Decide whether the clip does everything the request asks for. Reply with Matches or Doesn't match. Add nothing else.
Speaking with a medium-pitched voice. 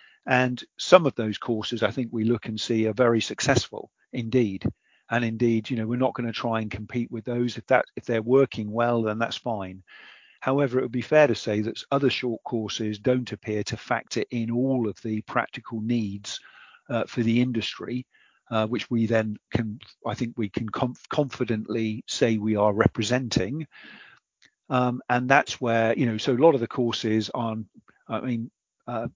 Doesn't match